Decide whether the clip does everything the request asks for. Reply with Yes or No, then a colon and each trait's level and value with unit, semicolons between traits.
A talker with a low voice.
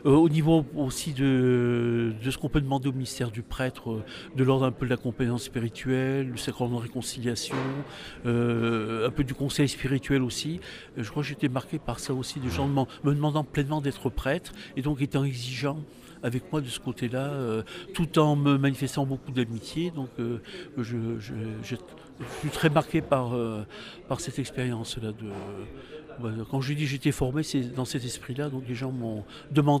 Yes: low, 130 Hz